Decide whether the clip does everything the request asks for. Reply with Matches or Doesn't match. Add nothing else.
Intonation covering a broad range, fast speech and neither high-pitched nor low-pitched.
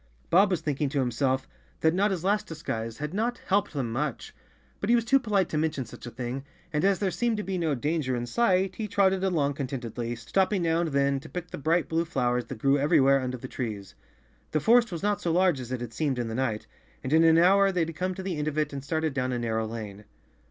Matches